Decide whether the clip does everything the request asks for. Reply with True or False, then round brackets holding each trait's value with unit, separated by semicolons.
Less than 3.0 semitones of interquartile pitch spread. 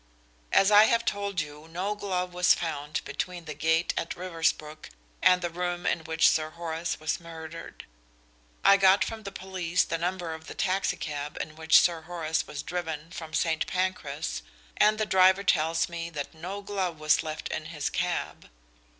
True (2.6 semitones)